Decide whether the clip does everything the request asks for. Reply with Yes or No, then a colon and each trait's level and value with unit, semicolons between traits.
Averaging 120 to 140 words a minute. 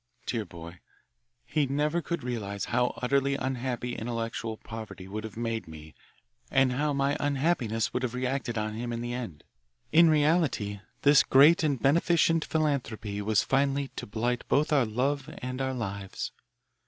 No: average, 155 wpm